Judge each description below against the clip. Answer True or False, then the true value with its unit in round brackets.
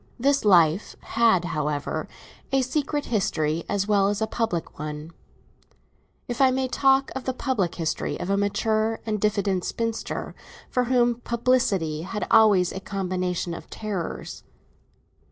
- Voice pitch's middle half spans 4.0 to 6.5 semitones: True (5.1 semitones)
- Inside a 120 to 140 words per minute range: True (135 wpm)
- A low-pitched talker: False (210 Hz)